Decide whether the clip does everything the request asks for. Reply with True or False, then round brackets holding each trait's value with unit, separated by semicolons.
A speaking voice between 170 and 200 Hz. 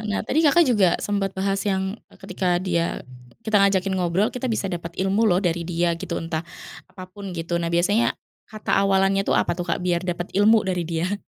True (190 Hz)